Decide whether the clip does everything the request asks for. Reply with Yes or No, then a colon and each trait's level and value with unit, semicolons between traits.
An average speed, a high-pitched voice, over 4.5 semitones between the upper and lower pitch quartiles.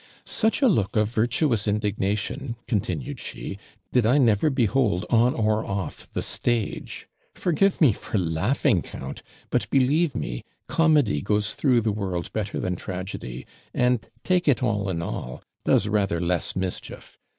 No: average, 150 wpm; low, 110 Hz; average, 4.9 semitones